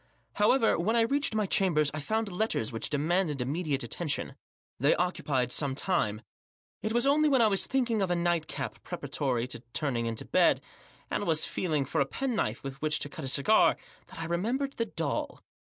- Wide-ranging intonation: Yes, wide, 7.7 semitones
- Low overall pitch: No, medium, 170 Hz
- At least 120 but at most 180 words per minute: No, average, 190 wpm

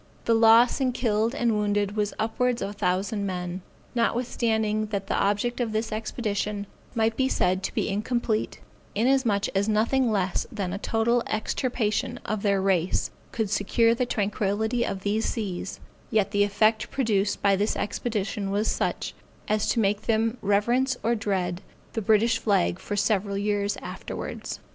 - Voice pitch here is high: Yes, high, 215 Hz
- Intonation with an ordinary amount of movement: No, narrow, 2.3 semitones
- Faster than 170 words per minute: No, average, 160 wpm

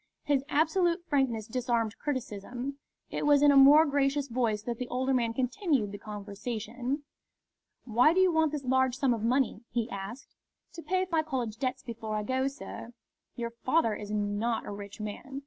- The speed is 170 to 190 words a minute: Yes, average, 180 wpm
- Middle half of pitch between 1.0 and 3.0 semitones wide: No, average, 4.0 semitones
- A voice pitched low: No, very high, 255 Hz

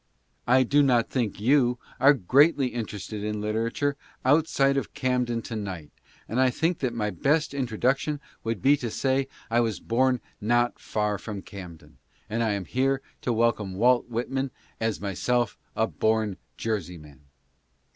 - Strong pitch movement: No, average, 3.8 semitones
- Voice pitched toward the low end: Yes, low, 120 Hz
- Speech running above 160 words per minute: No, average, 155 wpm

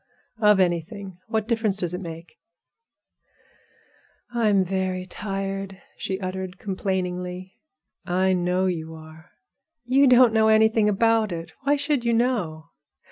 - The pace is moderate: No, slow, 125 wpm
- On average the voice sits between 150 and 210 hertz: Yes, high, 190 Hz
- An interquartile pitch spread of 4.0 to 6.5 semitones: No, average, 3.5 semitones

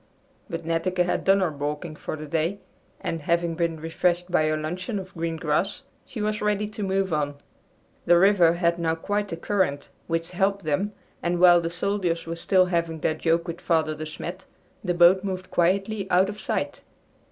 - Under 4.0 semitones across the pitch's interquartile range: Yes, average, 2.7 semitones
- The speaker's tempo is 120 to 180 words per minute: No, average, 190 wpm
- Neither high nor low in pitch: Yes, medium, 175 Hz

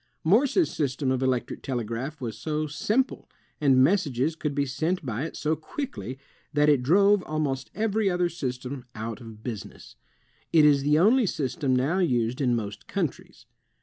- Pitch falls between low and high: Yes, medium, 145 Hz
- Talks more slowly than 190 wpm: Yes, average, 160 wpm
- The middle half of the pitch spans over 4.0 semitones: Yes, average, 5.0 semitones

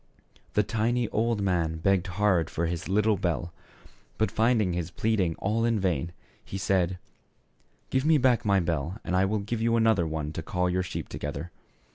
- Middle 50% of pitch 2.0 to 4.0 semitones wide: No, average, 4.4 semitones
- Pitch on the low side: Yes, very low, 95 Hz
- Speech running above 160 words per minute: Yes, average, 180 wpm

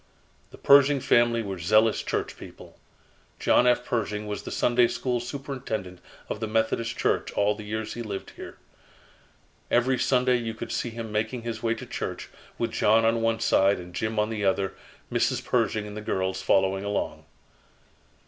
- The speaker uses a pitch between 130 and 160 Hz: No, low, 110 Hz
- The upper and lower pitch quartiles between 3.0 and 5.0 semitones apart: No, narrow, 2.4 semitones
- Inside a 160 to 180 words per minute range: Yes, average, 175 wpm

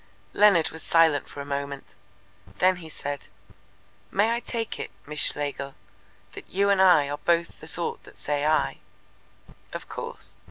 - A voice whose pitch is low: No, medium, 160 Hz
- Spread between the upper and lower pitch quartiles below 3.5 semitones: No, average, 4.5 semitones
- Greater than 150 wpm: Yes, average, 160 wpm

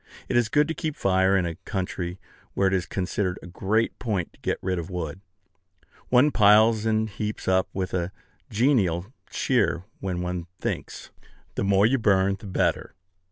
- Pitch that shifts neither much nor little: Yes, average, 3.3 semitones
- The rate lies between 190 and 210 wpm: No, average, 175 wpm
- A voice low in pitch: Yes, very low, 95 Hz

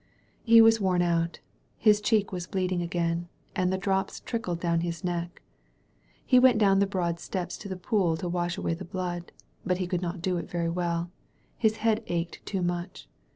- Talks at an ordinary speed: No, fast, 210 wpm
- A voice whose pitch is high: No, medium, 180 Hz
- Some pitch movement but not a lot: No, narrow, 2.2 semitones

